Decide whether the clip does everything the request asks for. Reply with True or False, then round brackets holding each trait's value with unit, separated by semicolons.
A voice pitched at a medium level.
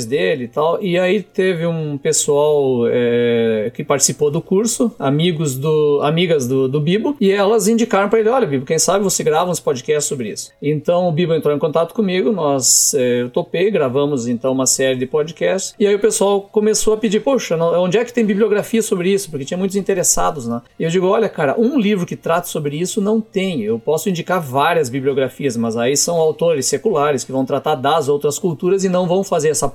True (175 Hz)